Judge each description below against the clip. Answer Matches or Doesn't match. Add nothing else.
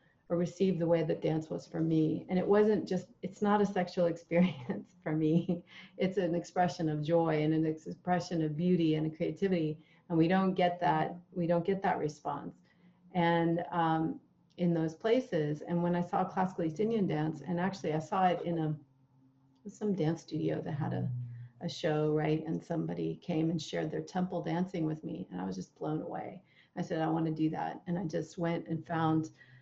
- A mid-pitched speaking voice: Matches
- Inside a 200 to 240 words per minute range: Matches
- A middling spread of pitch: Doesn't match